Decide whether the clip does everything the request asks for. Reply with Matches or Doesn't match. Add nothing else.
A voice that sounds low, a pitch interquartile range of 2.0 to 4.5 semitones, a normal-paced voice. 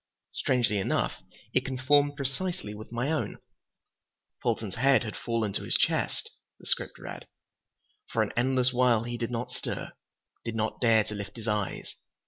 Matches